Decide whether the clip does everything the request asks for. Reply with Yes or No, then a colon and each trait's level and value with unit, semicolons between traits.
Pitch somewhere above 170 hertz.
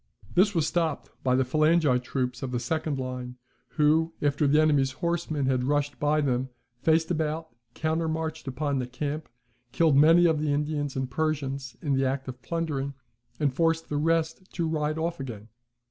No: medium, 150 Hz